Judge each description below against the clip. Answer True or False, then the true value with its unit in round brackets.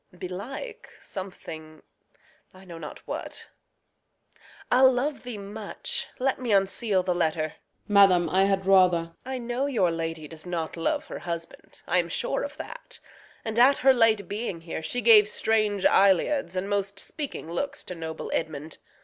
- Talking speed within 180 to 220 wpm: False (165 wpm)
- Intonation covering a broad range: True (6.2 semitones)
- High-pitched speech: True (195 Hz)